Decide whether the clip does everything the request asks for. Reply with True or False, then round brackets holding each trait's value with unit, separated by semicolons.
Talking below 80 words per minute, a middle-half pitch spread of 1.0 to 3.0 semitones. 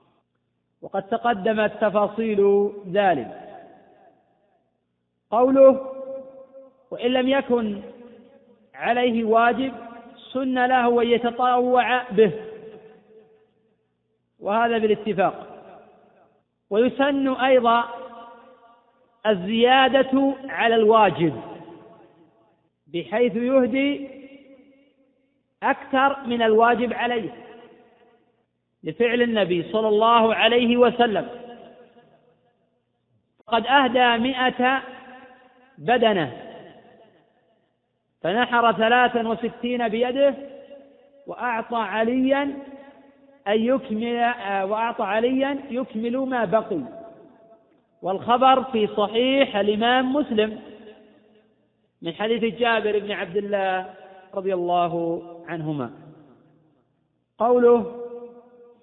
True (65 wpm; 2.7 semitones)